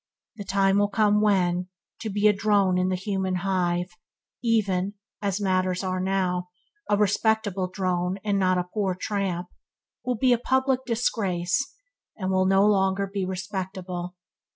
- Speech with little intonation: Yes, narrow, 2.2 semitones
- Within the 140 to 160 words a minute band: Yes, average, 155 wpm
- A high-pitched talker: Yes, high, 195 Hz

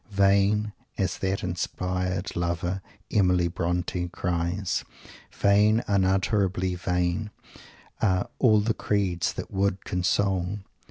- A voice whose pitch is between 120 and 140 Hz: No, very low, 95 Hz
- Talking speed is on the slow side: Yes, slow, 100 wpm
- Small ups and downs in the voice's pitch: Yes, narrow, 2.1 semitones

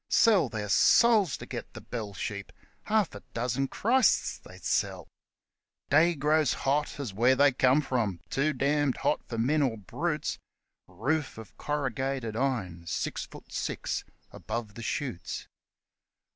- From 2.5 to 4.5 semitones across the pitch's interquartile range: No, average, 5.0 semitones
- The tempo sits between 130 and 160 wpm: Yes, average, 145 wpm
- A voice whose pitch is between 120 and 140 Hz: Yes, low, 135 Hz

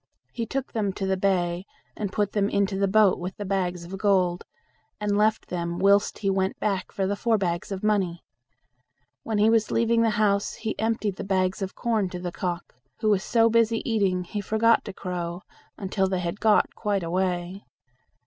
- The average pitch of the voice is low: No, high, 195 Hz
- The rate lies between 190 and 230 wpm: Yes, average, 195 wpm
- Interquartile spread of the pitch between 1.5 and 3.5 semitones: Yes, narrow, 2.6 semitones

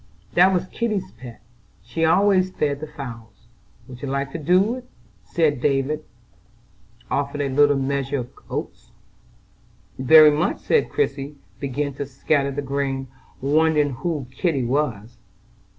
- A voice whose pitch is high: No, medium, 140 Hz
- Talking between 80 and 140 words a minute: Yes, slow, 135 wpm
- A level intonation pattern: No, average, 3.2 semitones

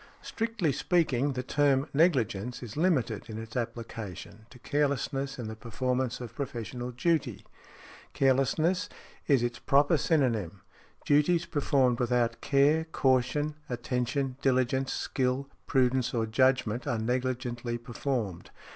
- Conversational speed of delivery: No, slow, 120 wpm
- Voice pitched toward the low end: Yes, low, 130 Hz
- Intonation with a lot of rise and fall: No, average, 3.1 semitones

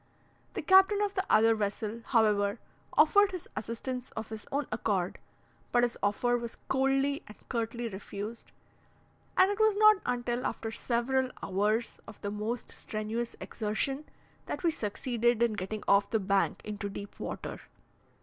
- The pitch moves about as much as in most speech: Yes, average, 3.9 semitones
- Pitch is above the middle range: Yes, high, 230 Hz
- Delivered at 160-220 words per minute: No, average, 150 wpm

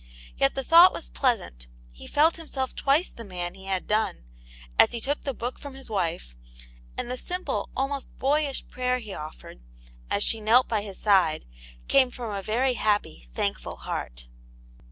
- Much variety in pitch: Yes, wide, 5.9 semitones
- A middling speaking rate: Yes, average, 175 wpm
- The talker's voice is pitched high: Yes, high, 230 Hz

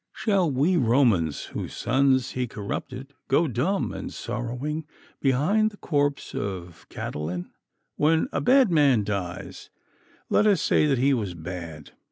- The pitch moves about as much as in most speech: No, wide, 7.3 semitones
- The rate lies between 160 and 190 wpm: No, average, 145 wpm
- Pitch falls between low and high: No, low, 130 Hz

